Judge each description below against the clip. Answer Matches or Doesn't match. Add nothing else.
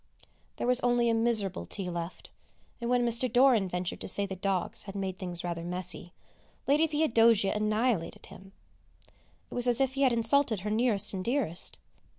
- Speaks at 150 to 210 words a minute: Matches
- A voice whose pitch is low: Doesn't match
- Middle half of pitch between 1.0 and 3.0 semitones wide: Doesn't match